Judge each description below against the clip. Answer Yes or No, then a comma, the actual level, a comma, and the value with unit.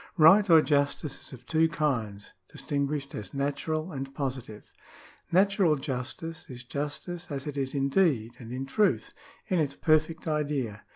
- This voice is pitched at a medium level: Yes, medium, 145 Hz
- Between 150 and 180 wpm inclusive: Yes, average, 160 wpm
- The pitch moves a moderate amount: Yes, average, 3.1 semitones